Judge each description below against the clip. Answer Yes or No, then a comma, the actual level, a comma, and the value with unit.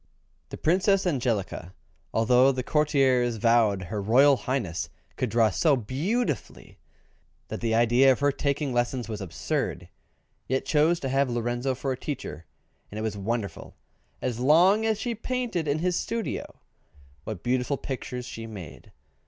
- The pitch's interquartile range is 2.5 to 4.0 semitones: No, average, 4.6 semitones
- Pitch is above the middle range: No, low, 130 Hz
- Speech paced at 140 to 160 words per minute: Yes, average, 150 wpm